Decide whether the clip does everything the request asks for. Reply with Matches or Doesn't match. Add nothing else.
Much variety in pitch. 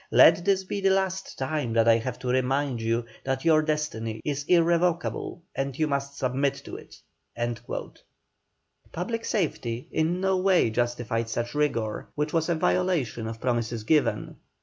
Matches